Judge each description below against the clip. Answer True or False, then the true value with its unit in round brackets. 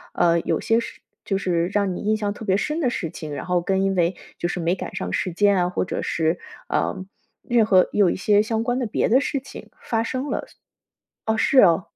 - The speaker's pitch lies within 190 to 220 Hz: True (200 Hz)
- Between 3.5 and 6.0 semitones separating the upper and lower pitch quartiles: True (4.1 semitones)